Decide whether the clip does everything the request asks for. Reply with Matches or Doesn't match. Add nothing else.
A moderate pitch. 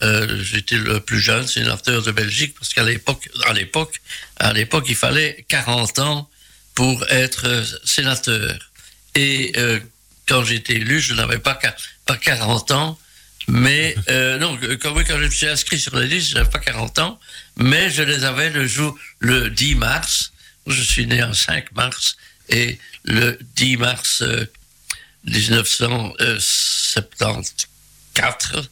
Doesn't match